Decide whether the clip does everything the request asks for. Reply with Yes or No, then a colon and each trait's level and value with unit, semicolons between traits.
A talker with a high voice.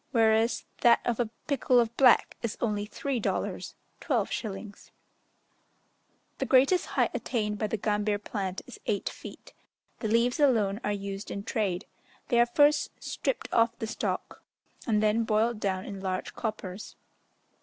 Yes: high, 220 Hz